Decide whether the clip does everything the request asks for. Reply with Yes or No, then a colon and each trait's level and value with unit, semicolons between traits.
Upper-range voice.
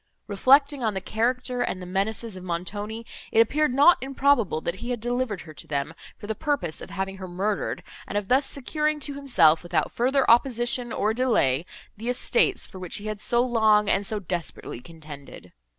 Yes: high, 220 Hz